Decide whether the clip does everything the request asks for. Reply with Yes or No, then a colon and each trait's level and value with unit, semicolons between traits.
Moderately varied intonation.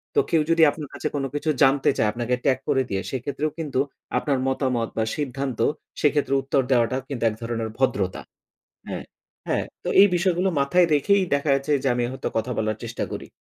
Yes: average, 3.5 semitones